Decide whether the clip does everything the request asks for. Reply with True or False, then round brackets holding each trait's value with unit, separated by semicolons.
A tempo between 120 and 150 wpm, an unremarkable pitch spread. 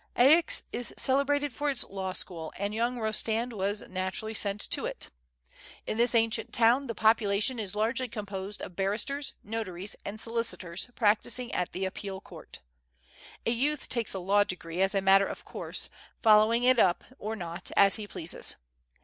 False (165 wpm; 3.6 semitones)